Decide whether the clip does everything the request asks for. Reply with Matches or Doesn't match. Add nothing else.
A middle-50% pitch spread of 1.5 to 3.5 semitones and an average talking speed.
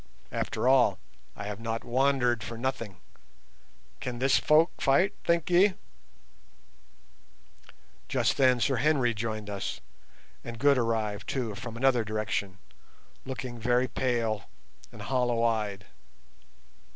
Doesn't match